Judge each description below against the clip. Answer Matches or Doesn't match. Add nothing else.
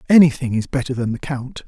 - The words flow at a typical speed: Doesn't match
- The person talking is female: Doesn't match